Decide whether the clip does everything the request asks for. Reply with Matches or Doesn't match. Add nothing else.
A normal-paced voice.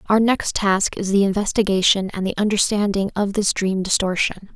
Matches